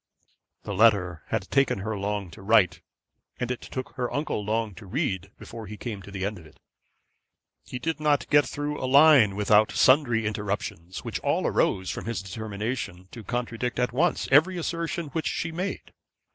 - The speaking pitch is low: Yes, low, 115 Hz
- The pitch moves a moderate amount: No, wide, 5.9 semitones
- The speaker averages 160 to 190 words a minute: Yes, average, 180 wpm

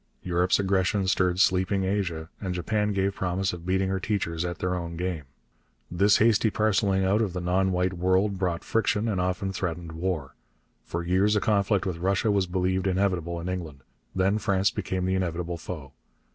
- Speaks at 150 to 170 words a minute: No, average, 180 wpm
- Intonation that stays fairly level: Yes, narrow, 1.8 semitones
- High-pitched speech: No, very low, 95 Hz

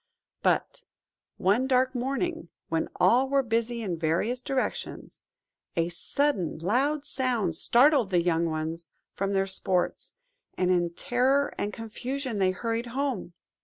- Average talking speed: No, slow, 130 wpm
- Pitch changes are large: Yes, wide, 6.6 semitones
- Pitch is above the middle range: Yes, high, 230 Hz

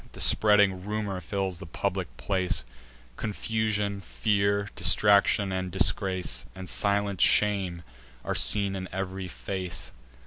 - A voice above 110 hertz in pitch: No, low, 100 Hz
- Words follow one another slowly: Yes, slow, 115 wpm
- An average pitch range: No, narrow, 1.6 semitones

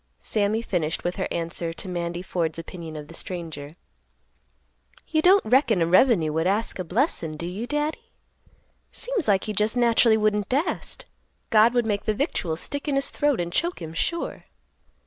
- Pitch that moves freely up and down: Yes, wide, 6.4 semitones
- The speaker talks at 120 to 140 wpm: No, average, 175 wpm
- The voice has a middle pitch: No, high, 205 Hz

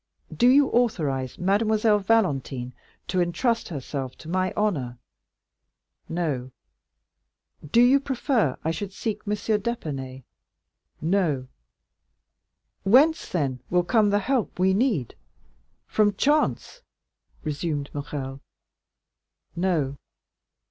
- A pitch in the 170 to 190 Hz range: Yes, medium, 185 Hz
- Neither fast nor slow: No, slow, 95 wpm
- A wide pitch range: Yes, wide, 7.7 semitones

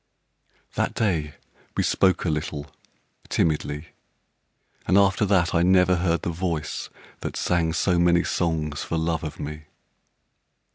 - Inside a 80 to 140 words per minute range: Yes, slow, 135 wpm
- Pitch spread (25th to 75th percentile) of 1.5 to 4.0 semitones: Yes, average, 2.8 semitones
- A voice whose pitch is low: Yes, very low, 85 Hz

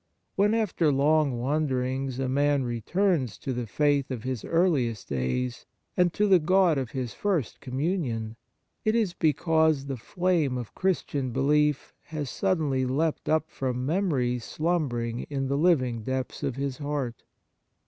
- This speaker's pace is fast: No, average, 150 wpm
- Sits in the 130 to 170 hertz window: Yes, medium, 140 Hz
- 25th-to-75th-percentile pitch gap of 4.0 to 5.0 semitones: Yes, average, 4.3 semitones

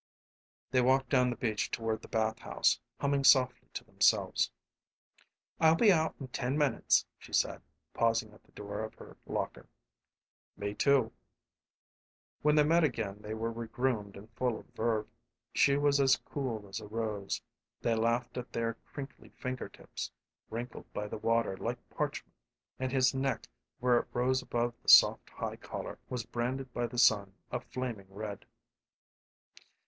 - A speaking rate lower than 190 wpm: Yes, average, 165 wpm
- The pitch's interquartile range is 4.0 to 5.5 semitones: No, average, 3.1 semitones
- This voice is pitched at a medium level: No, low, 120 Hz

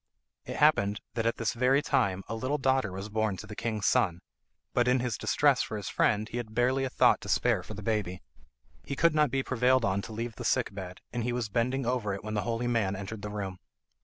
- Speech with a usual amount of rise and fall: Yes, average, 3.5 semitones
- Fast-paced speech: Yes, fast, 245 wpm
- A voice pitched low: Yes, low, 115 Hz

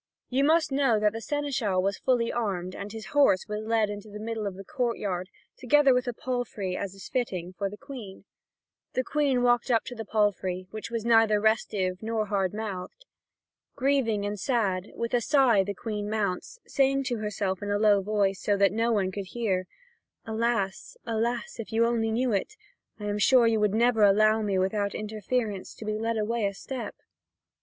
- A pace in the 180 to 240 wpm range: Yes, average, 195 wpm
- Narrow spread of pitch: No, average, 3.0 semitones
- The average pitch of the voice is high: Yes, high, 215 Hz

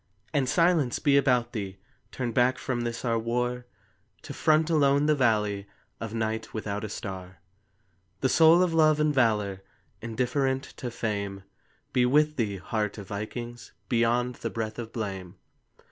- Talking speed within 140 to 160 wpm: Yes, average, 155 wpm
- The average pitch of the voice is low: Yes, low, 120 Hz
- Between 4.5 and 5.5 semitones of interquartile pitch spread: No, average, 3.8 semitones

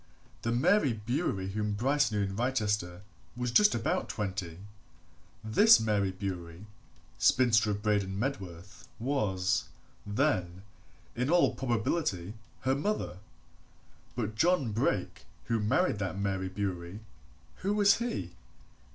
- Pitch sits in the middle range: No, low, 105 Hz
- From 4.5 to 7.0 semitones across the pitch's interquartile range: Yes, average, 5.3 semitones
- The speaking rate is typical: No, slow, 115 wpm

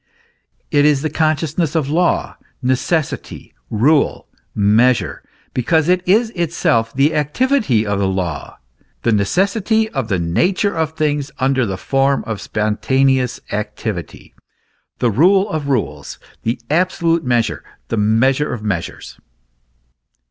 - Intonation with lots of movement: Yes, wide, 6.6 semitones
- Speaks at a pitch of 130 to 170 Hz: Yes, low, 135 Hz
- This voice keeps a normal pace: No, slow, 125 wpm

